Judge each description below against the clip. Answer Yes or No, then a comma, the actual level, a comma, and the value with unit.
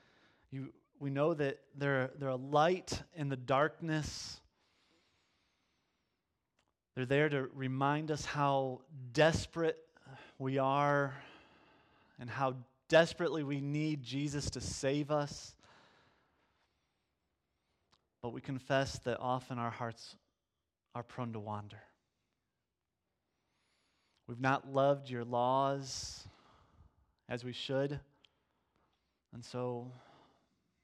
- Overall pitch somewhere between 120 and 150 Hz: Yes, low, 135 Hz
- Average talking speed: No, slow, 95 wpm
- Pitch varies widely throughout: No, average, 2.9 semitones